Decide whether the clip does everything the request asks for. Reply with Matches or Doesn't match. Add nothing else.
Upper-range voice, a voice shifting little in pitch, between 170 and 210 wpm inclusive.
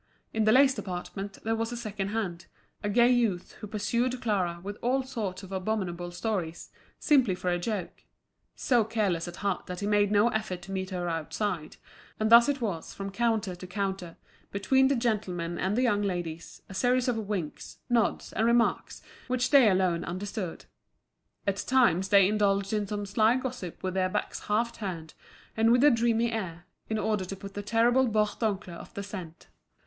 Doesn't match